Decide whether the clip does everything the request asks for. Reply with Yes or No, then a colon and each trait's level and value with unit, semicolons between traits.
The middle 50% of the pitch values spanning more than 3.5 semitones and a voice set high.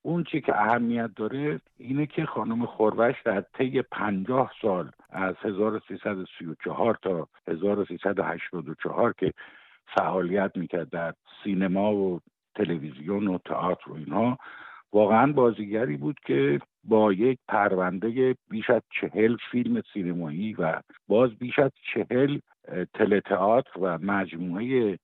No: average, 4.7 semitones; low, 105 Hz